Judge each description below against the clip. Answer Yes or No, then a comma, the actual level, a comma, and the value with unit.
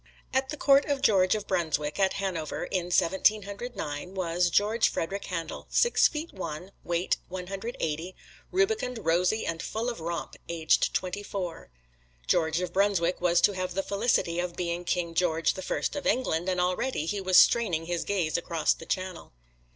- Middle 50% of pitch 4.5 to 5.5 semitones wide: No, average, 3.3 semitones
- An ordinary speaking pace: Yes, average, 180 wpm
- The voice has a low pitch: No, medium, 185 Hz